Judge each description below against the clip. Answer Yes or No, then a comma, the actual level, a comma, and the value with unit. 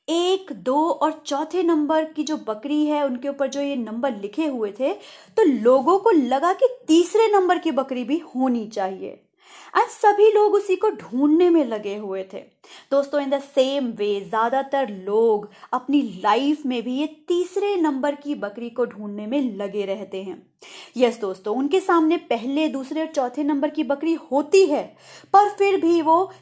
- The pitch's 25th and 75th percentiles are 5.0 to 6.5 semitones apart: Yes, average, 5.3 semitones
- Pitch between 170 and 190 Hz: No, very high, 285 Hz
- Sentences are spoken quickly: No, average, 175 wpm